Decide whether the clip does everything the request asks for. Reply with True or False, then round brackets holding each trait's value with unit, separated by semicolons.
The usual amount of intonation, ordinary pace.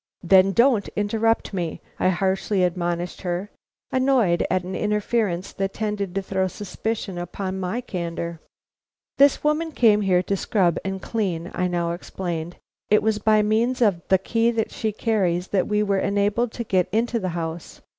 True (3.5 semitones; 165 wpm)